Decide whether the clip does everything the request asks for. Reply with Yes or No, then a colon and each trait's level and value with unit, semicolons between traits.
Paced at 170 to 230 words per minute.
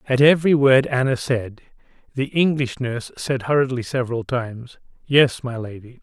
No: average, 150 wpm